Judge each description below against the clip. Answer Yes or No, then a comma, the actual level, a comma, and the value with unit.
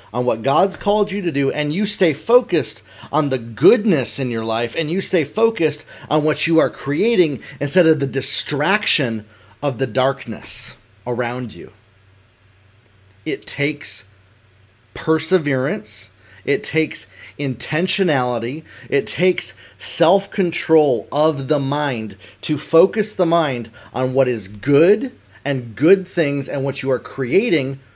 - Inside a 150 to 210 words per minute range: No, slow, 135 wpm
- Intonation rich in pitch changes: Yes, wide, 6.0 semitones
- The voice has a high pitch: No, low, 135 Hz